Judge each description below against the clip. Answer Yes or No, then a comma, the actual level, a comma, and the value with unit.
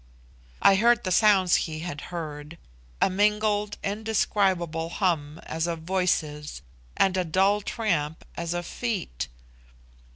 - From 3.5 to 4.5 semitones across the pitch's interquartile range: Yes, average, 4.2 semitones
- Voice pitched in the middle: Yes, medium, 180 Hz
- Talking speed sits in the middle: No, slow, 125 wpm